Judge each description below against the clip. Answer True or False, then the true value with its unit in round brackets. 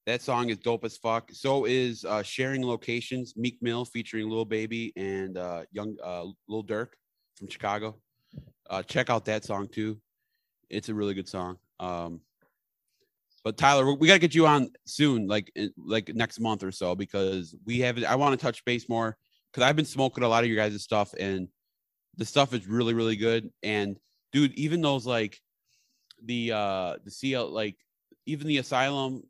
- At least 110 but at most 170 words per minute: False (180 wpm)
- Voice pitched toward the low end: True (115 Hz)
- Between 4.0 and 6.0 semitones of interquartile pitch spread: False (3.5 semitones)